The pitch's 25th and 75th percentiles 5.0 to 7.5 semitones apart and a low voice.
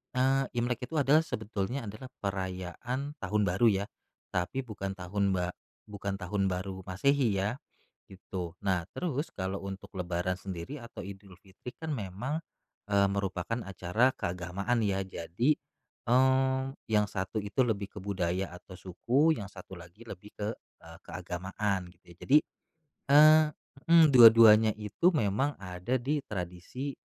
Yes: average, 5.3 semitones; low, 100 Hz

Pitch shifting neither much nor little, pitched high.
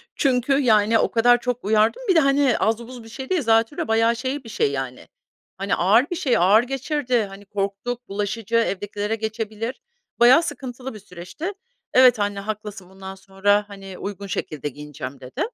Yes: average, 3.9 semitones; high, 220 Hz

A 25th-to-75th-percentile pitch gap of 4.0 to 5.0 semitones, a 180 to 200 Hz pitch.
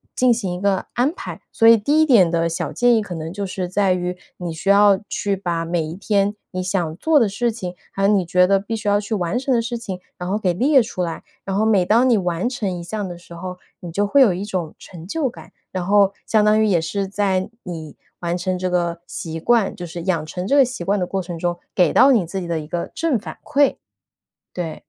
No: average, 3.6 semitones; high, 190 Hz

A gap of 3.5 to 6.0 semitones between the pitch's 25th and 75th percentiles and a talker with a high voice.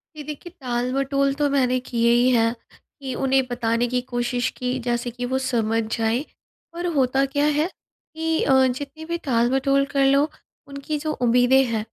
No: narrow, 2.5 semitones; very high, 260 Hz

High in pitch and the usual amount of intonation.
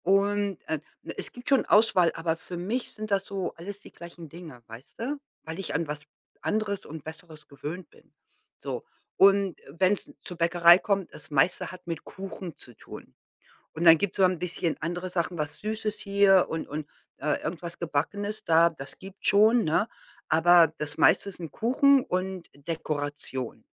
No: medium, 175 Hz; average, 3.8 semitones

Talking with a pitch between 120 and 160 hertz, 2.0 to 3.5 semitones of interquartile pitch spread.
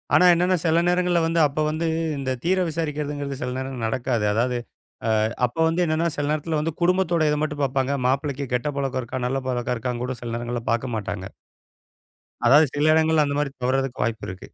No: medium, 140 Hz; average, 4.1 semitones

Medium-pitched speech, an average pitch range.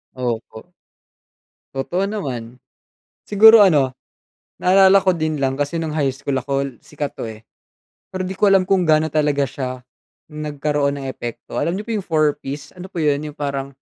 Yes: medium, 150 Hz; average, 4.9 semitones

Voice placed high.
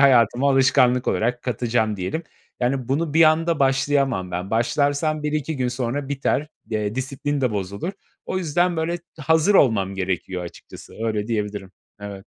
No: low, 130 Hz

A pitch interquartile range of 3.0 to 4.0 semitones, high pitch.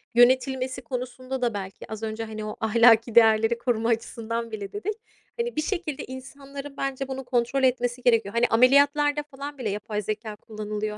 Yes: average, 3.4 semitones; high, 245 Hz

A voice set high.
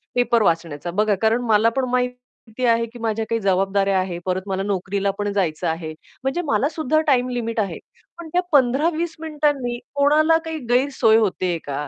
Yes: high, 230 Hz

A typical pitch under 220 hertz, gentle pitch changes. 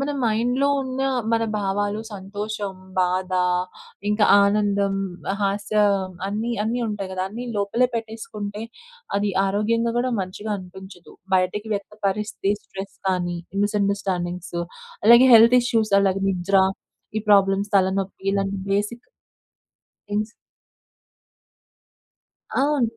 Yes: high, 205 Hz; narrow, 2.3 semitones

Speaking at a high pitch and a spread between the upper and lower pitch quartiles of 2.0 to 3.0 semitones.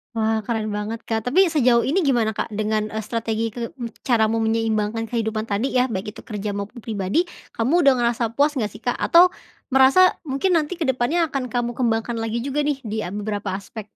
No: high, 230 Hz; average, 3.5 semitones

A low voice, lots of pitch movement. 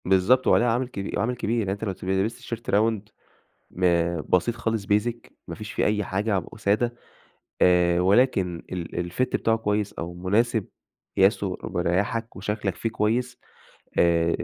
No: low, 105 Hz; average, 3.8 semitones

